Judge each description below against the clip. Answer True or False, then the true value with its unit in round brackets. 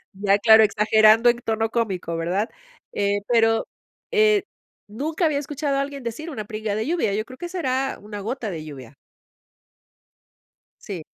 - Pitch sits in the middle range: False (225 Hz)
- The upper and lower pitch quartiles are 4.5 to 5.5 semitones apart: True (5.2 semitones)